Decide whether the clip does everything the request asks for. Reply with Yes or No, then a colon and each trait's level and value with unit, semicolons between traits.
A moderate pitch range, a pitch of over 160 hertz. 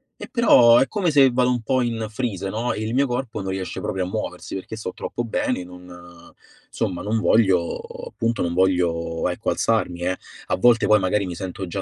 No: average, 4.8 semitones; low, 105 Hz